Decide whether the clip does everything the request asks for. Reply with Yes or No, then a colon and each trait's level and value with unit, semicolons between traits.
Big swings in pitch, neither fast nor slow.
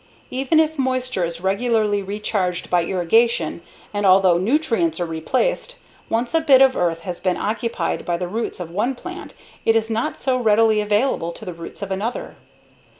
Yes: wide, 5.8 semitones; average, 175 wpm